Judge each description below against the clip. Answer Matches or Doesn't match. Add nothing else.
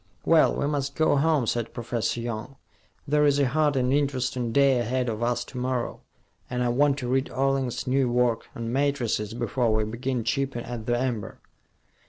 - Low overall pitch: Matches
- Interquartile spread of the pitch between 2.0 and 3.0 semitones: Matches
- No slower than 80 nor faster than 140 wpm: Doesn't match